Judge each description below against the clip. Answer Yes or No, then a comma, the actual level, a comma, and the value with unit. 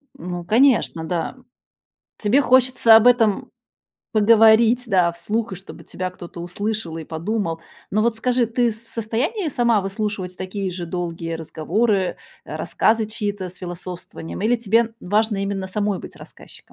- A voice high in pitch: Yes, high, 210 Hz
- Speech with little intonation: No, average, 4.1 semitones